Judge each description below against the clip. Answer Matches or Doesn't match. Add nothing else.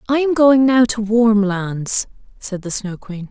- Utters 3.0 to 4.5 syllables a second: Matches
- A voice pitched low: Doesn't match